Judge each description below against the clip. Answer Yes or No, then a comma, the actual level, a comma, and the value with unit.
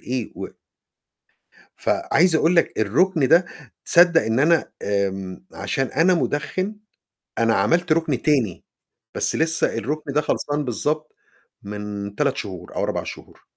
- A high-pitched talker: No, medium, 145 Hz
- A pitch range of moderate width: No, wide, 6.9 semitones